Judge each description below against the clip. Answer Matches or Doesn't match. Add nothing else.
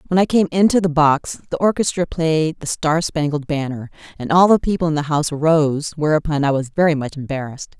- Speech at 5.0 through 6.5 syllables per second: Matches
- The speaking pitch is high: Doesn't match